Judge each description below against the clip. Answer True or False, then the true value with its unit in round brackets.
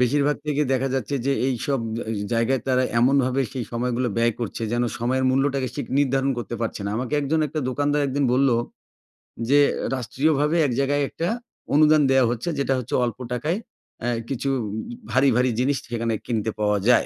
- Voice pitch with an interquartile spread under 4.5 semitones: True (2.8 semitones)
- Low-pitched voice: True (130 Hz)